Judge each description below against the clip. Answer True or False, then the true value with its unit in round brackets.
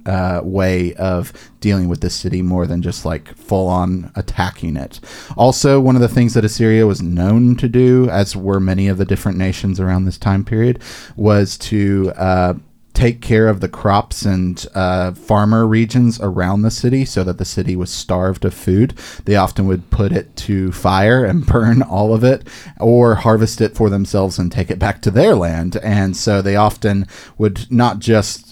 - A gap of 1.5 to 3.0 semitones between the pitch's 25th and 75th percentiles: False (3.4 semitones)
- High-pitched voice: False (100 Hz)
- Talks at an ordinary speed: True (190 wpm)